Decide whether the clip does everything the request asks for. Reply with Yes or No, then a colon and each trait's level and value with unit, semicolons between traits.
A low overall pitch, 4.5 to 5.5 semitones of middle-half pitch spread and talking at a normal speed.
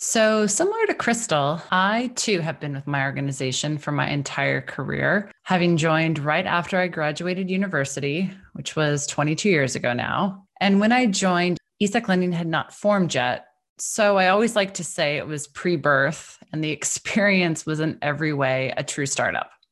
No: medium, 165 Hz; average, 5.1 semitones; average, 175 wpm